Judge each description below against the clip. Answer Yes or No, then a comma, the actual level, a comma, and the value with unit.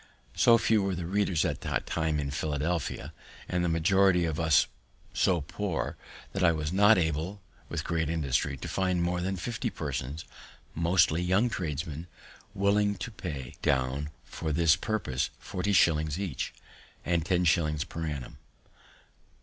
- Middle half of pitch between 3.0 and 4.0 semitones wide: Yes, average, 3.7 semitones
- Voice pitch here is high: No, very low, 85 Hz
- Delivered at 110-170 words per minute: Yes, average, 150 wpm